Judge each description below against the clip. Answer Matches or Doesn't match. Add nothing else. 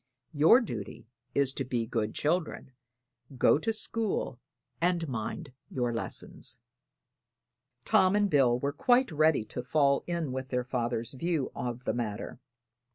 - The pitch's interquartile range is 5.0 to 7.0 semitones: Matches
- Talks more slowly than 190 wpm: Matches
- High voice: Doesn't match